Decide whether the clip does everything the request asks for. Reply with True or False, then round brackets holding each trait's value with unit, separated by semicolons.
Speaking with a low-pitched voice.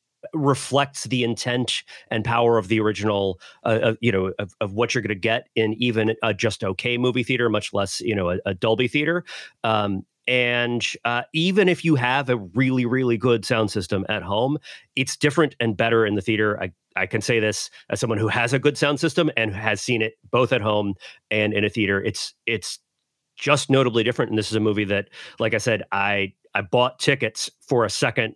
True (115 Hz)